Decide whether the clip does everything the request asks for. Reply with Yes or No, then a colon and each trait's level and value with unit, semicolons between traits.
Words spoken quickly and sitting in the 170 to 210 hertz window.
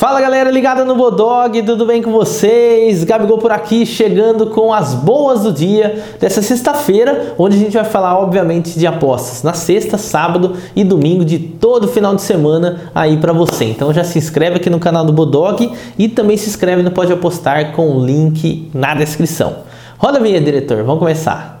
Yes: fast, 190 wpm; medium, 185 Hz